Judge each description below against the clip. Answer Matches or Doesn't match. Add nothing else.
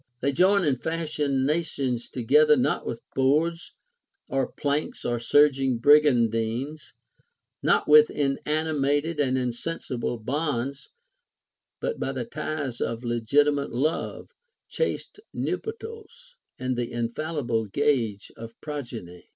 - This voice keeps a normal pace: Doesn't match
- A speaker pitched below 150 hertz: Matches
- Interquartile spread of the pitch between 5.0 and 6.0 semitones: Doesn't match